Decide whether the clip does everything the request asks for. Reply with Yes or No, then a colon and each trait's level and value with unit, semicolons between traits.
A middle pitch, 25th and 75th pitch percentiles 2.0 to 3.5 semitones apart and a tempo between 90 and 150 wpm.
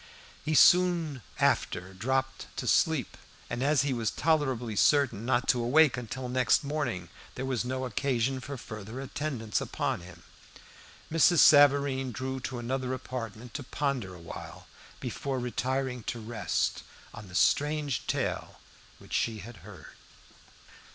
No: low, 130 Hz; average, 3.2 semitones; average, 140 wpm